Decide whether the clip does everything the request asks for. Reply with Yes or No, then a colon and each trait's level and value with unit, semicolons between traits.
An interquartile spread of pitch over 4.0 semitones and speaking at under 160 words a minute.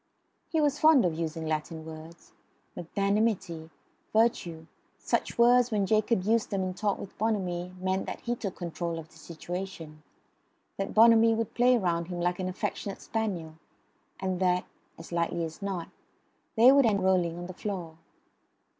No: average, 4.4 semitones; average, 165 wpm